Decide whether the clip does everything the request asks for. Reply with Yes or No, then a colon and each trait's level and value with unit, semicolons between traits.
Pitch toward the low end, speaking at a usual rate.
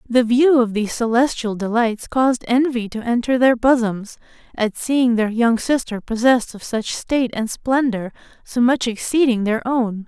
No: high, 235 Hz; average, 165 wpm